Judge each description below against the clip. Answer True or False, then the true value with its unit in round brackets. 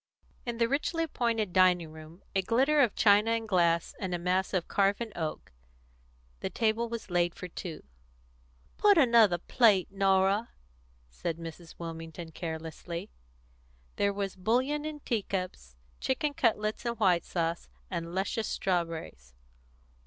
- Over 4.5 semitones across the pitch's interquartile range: True (5.2 semitones)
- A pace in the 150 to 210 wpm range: False (135 wpm)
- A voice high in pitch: True (195 Hz)